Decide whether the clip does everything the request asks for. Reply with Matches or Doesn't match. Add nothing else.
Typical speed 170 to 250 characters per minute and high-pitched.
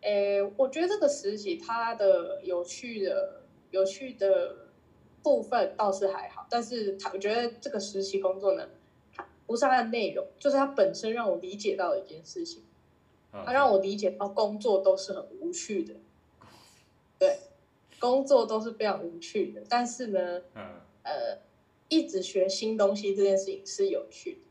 Matches